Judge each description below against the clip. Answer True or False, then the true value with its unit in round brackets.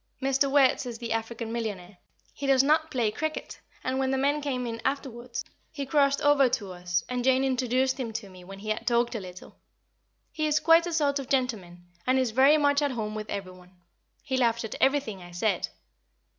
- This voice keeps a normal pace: False (210 wpm)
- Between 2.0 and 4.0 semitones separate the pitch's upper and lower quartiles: False (4.4 semitones)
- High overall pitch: True (250 Hz)